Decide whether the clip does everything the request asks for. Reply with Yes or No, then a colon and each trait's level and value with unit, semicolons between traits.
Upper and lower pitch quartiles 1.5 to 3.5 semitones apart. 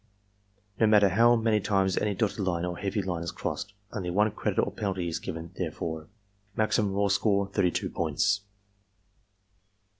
Yes: average, 2.9 semitones